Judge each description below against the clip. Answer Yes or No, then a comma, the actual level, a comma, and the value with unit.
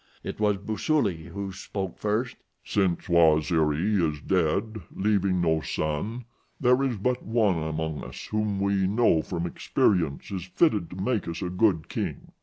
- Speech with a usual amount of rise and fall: Yes, average, 4.4 semitones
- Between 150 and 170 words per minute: Yes, average, 155 wpm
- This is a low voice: Yes, very low, 95 Hz